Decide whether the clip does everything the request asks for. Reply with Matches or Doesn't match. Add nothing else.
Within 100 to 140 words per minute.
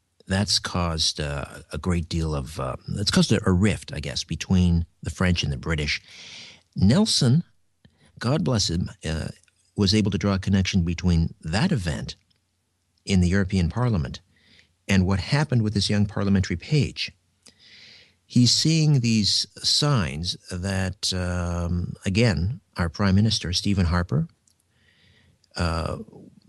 Matches